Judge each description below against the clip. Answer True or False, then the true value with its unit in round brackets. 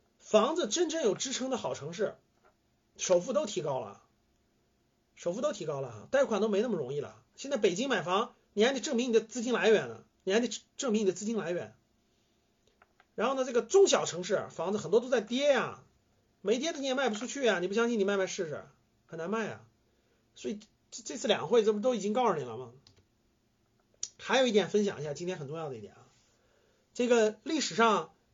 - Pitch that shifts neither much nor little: False (6.4 semitones)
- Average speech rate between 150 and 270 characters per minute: False (295 characters per minute)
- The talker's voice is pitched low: False (220 Hz)